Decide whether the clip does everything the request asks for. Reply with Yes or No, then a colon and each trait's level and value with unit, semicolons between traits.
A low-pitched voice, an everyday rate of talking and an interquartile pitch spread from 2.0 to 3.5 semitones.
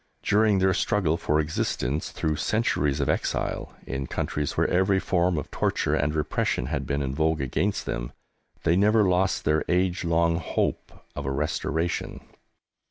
No: very low, 80 Hz; average, 160 wpm; average, 4.3 semitones